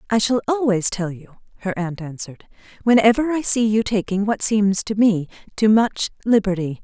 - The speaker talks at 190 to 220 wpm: No, average, 175 wpm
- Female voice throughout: Yes, female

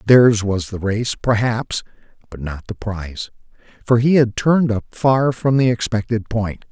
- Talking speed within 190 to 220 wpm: No, average, 170 wpm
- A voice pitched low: Yes, low, 115 Hz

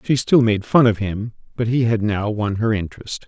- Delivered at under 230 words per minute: No, fast, 240 wpm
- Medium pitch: No, low, 110 Hz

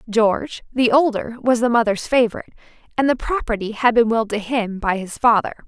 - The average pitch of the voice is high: Yes, high, 230 Hz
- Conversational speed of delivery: Yes, average, 190 wpm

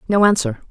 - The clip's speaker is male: No, female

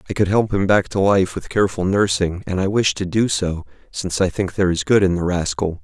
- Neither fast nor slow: No, fast, 255 wpm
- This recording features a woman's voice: No, male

